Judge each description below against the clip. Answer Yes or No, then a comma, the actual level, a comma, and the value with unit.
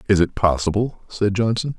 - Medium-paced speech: Yes, average, 170 wpm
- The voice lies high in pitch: No, low, 100 Hz